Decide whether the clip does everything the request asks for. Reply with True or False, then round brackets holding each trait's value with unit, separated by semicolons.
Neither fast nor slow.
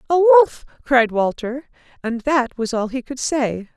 True (175 wpm)